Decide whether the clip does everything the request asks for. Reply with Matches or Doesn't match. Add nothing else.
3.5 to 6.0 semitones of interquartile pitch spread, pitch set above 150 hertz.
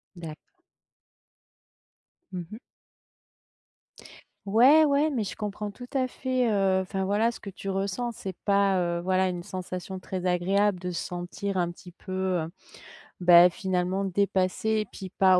Doesn't match